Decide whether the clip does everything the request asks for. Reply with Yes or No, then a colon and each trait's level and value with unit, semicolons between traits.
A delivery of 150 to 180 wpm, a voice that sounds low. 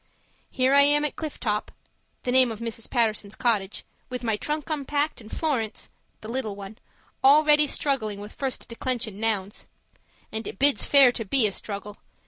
No: average, 170 wpm; high, 240 Hz